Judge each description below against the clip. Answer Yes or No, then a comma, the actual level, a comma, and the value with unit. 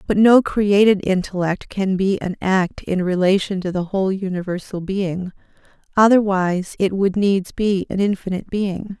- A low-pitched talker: No, high, 190 Hz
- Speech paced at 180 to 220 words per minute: No, average, 155 wpm